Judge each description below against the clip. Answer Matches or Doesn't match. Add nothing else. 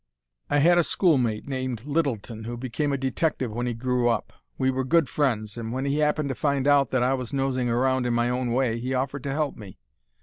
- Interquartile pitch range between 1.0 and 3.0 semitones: Matches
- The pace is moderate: Doesn't match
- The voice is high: Doesn't match